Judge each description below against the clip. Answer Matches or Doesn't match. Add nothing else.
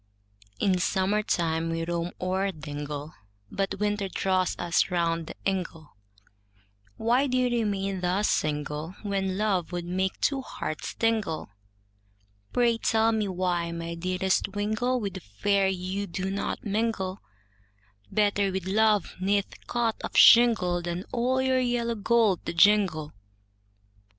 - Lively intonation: Doesn't match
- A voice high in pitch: Matches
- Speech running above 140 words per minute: Doesn't match